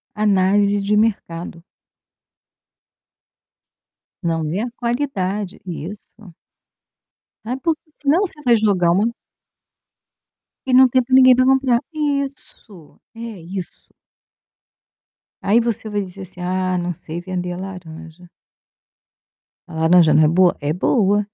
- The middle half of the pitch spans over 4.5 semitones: Yes, average, 5.2 semitones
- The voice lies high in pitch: Yes, high, 195 Hz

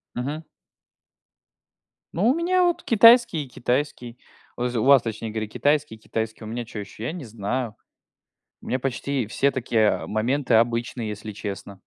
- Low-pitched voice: Yes, low, 120 Hz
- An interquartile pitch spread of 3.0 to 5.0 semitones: Yes, average, 4.7 semitones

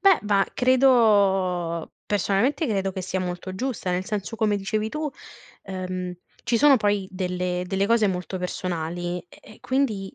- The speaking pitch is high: Yes, high, 195 Hz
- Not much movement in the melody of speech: No, average, 3.4 semitones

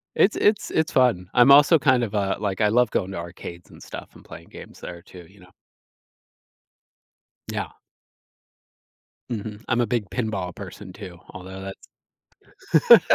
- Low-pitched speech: Yes, low, 105 Hz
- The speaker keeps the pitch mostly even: No, average, 4.8 semitones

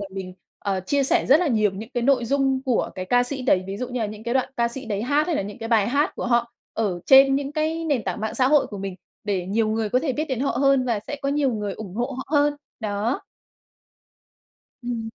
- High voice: Yes, high, 240 Hz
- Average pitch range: Yes, average, 4.6 semitones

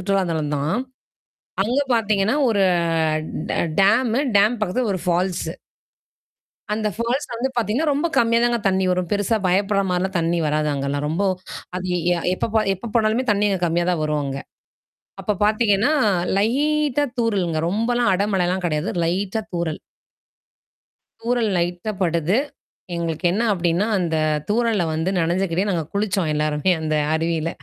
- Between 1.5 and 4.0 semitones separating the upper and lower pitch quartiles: No, average, 4.6 semitones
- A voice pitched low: No, high, 195 Hz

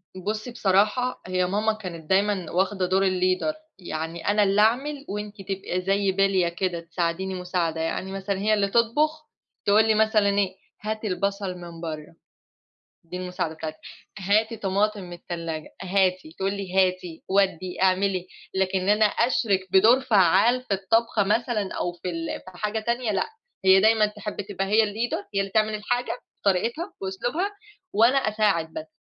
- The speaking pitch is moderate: No, high, 195 Hz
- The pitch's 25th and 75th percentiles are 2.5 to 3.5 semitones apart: Yes, average, 2.9 semitones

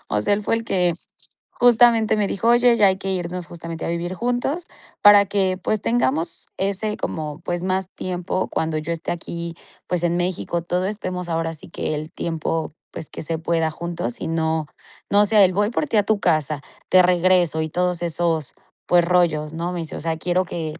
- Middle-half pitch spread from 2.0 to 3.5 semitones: Yes, average, 3.0 semitones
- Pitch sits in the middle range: Yes, medium, 175 Hz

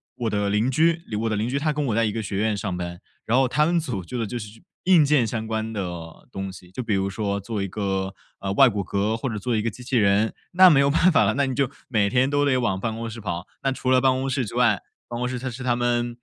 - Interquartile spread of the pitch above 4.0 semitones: Yes, average, 4.4 semitones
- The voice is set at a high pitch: No, low, 115 Hz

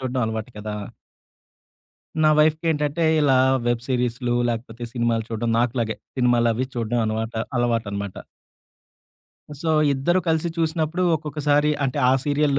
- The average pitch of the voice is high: No, low, 125 Hz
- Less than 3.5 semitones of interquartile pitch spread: No, average, 4.5 semitones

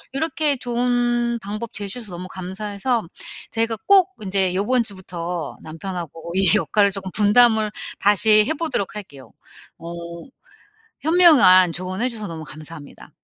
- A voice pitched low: No, high, 205 Hz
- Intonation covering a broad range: No, average, 4.7 semitones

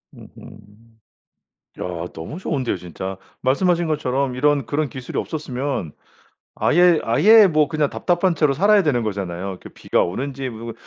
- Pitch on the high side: No, medium, 140 Hz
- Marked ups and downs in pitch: Yes, wide, 5.9 semitones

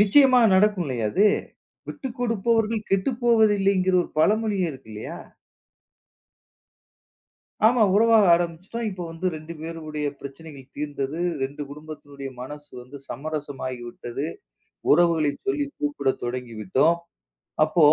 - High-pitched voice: No, medium, 165 Hz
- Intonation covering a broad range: Yes, wide, 6.8 semitones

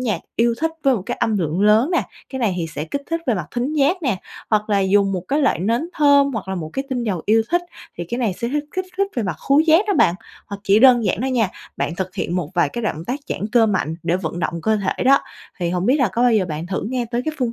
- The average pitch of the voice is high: Yes, high, 225 Hz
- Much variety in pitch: Yes, wide, 6.2 semitones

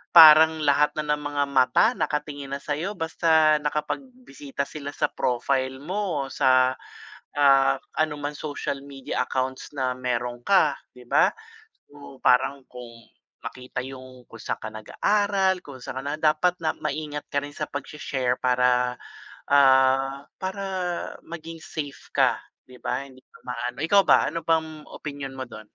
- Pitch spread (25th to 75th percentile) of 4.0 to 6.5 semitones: No, average, 3.2 semitones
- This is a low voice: No, medium, 145 Hz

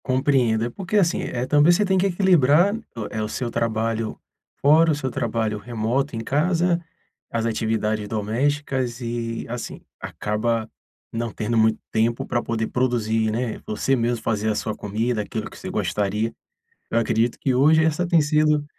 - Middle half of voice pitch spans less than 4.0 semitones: No, average, 4.7 semitones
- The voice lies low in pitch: Yes, low, 120 Hz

